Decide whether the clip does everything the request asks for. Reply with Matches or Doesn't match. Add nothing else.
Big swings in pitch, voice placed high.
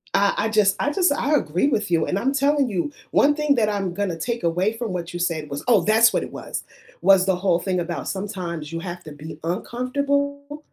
Matches